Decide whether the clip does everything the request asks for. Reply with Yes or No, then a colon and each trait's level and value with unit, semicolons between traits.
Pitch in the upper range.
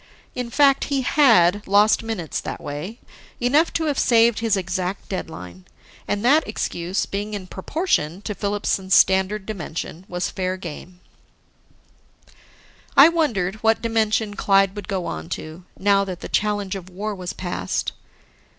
Yes: high, 200 Hz